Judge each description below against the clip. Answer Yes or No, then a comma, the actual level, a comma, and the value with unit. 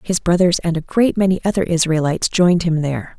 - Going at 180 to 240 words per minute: Yes, fast, 205 wpm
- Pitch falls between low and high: Yes, medium, 175 Hz